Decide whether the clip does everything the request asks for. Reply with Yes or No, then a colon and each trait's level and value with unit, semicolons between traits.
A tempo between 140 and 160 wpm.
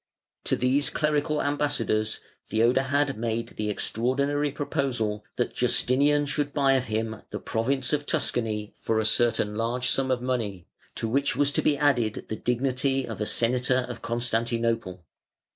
Yes: average, 150 wpm